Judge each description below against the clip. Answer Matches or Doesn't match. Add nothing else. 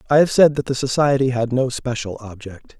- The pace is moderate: Doesn't match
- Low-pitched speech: Matches